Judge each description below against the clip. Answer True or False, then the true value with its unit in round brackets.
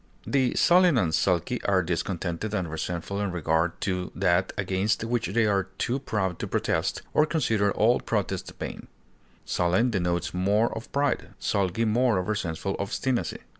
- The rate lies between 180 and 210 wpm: False (155 wpm)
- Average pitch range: True (4.2 semitones)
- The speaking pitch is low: True (100 Hz)